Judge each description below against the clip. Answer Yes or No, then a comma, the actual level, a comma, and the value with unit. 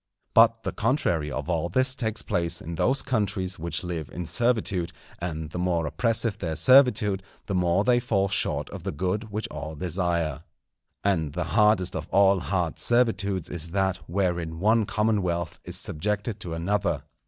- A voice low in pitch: Yes, very low, 95 Hz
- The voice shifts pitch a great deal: No, average, 4.1 semitones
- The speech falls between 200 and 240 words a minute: No, average, 165 wpm